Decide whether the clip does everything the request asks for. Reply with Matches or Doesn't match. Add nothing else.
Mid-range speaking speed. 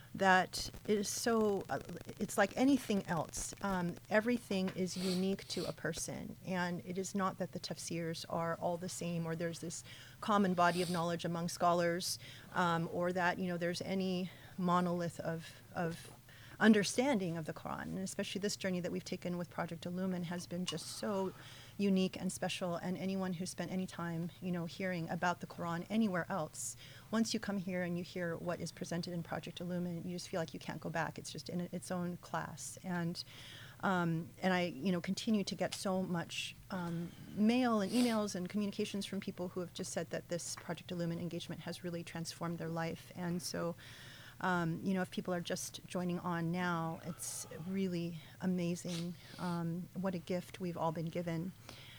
Matches